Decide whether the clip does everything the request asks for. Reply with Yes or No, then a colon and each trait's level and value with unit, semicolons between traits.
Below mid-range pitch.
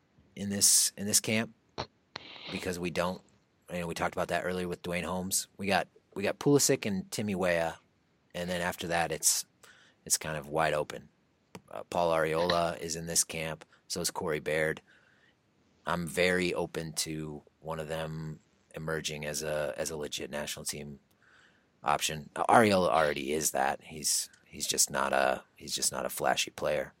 Yes: very low, 85 Hz